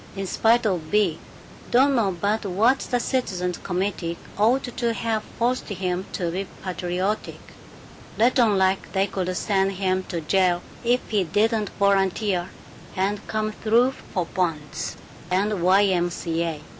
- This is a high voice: Yes, high, 195 Hz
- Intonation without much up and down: No, average, 3.2 semitones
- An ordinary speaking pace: Yes, average, 155 wpm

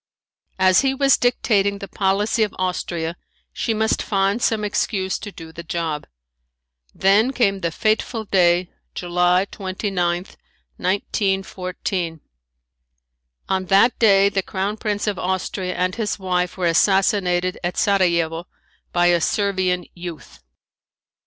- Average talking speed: No, slow, 125 wpm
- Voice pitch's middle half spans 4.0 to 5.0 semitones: No, narrow, 2.4 semitones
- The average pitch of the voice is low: No, high, 190 Hz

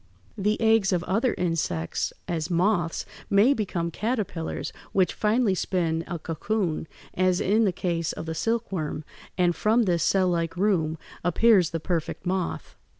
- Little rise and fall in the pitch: No, average, 4.0 semitones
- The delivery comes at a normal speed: Yes, average, 150 wpm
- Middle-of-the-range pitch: Yes, medium, 180 Hz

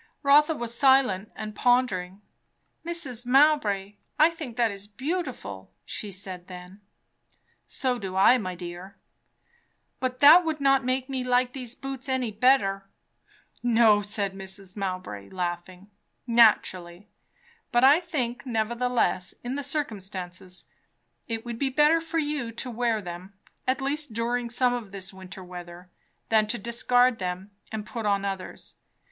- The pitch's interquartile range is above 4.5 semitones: Yes, average, 5.1 semitones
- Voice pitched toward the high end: Yes, high, 230 Hz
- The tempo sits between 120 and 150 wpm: Yes, average, 140 wpm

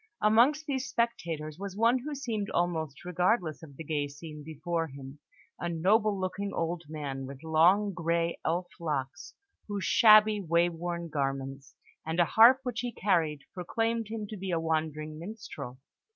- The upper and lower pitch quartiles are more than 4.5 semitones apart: Yes, average, 5.2 semitones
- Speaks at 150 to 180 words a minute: Yes, average, 160 wpm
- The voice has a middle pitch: Yes, medium, 170 Hz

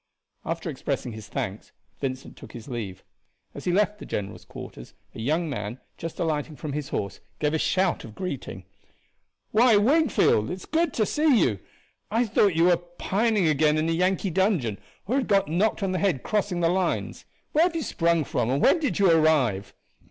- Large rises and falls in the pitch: Yes, wide, 7.1 semitones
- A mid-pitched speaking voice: Yes, medium, 170 Hz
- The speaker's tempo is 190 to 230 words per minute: Yes, average, 195 wpm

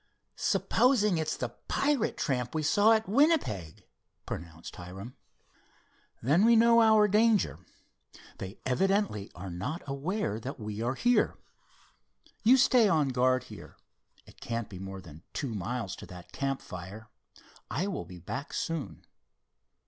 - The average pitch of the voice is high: No, low, 135 Hz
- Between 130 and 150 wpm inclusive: Yes, slow, 135 wpm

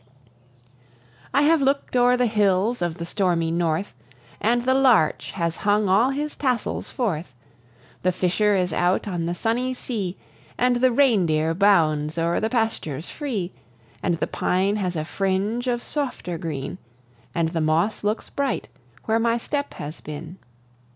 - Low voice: No, high, 200 Hz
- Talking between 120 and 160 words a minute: Yes, average, 155 wpm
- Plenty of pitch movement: Yes, wide, 6.3 semitones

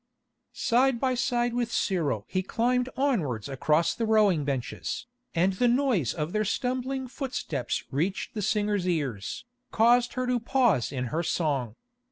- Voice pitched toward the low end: No, high, 210 Hz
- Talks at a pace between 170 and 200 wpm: No, average, 150 wpm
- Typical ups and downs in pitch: No, wide, 8.2 semitones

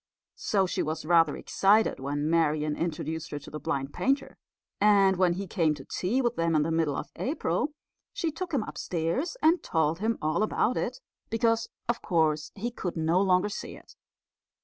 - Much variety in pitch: Yes, wide, 5.9 semitones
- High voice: No, medium, 175 Hz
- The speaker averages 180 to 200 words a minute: Yes, average, 185 wpm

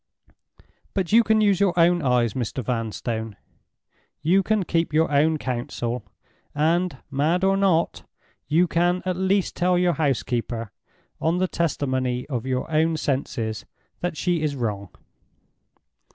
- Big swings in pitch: Yes, wide, 6.0 semitones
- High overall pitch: No, medium, 155 Hz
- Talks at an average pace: No, slow, 130 wpm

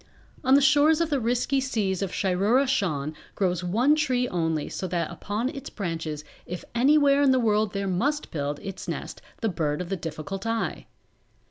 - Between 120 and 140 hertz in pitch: No, high, 205 Hz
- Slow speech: No, average, 185 wpm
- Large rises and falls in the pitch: Yes, wide, 6.9 semitones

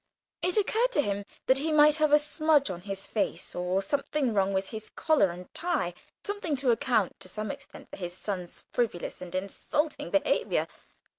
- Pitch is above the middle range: Yes, high, 235 Hz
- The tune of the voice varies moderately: No, wide, 7.8 semitones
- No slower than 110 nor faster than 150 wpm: No, average, 180 wpm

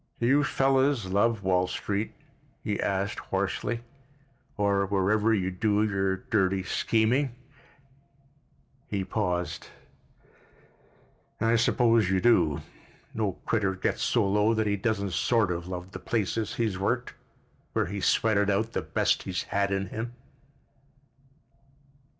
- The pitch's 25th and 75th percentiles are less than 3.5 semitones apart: Yes, average, 2.9 semitones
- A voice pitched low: Yes, low, 100 Hz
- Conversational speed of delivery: No, slow, 125 wpm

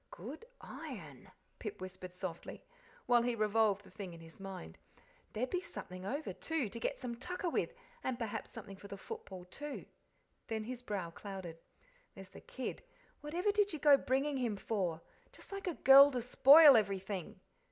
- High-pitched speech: Yes, high, 225 Hz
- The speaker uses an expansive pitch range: Yes, wide, 6.5 semitones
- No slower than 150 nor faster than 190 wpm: Yes, average, 175 wpm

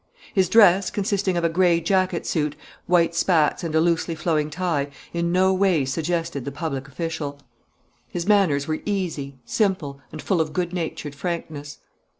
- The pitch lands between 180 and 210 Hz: No, medium, 170 Hz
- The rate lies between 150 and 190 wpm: Yes, average, 160 wpm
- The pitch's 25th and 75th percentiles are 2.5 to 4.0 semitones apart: Yes, average, 3.5 semitones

